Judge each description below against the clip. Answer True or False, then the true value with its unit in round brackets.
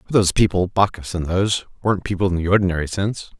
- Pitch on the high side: False (95 Hz)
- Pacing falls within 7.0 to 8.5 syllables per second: True (7.3 syllables/s)